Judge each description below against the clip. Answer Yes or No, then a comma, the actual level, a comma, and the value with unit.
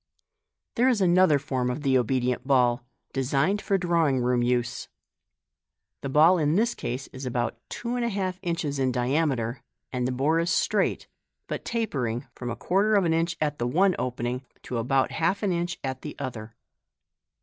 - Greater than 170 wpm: Yes, average, 180 wpm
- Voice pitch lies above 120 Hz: Yes, medium, 140 Hz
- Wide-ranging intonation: Yes, wide, 5.8 semitones